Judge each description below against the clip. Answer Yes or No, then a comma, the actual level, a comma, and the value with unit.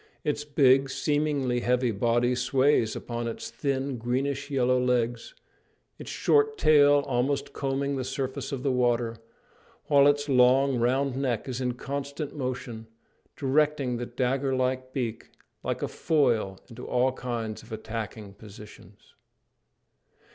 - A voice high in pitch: No, low, 130 Hz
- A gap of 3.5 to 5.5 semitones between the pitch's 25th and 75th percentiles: No, narrow, 2.5 semitones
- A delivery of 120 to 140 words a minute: Yes, slow, 135 wpm